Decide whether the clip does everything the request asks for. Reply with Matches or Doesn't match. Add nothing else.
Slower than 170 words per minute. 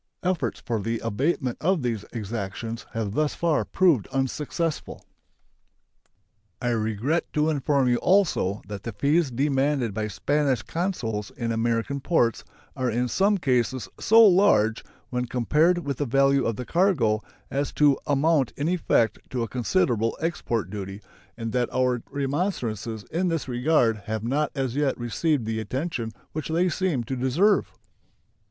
Matches